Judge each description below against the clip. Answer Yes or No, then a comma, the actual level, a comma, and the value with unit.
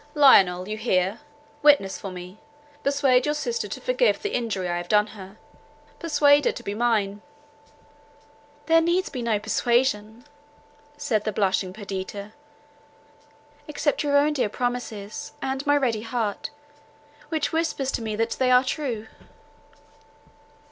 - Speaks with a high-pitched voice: Yes, high, 235 Hz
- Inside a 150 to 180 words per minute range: No, slow, 135 wpm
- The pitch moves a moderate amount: No, wide, 5.8 semitones